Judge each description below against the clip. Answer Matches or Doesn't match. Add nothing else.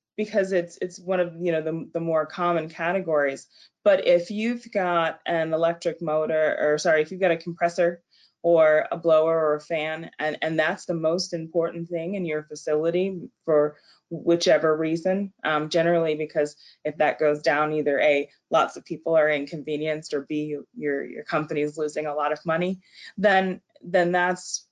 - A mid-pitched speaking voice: Matches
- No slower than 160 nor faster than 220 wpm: Matches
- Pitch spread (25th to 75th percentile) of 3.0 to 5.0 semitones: Doesn't match